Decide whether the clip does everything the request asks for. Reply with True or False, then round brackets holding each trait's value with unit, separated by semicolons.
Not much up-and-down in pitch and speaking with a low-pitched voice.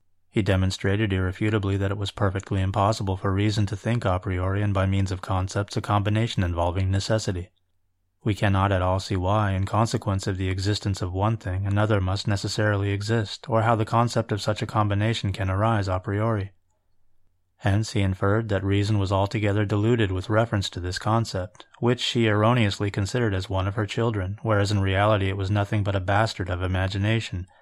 True (2.2 semitones; 100 Hz)